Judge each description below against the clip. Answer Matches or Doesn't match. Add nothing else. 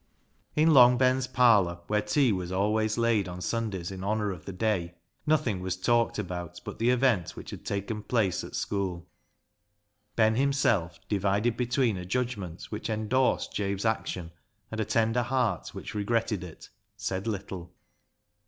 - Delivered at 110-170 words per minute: Matches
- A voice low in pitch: Matches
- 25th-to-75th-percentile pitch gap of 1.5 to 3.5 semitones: Doesn't match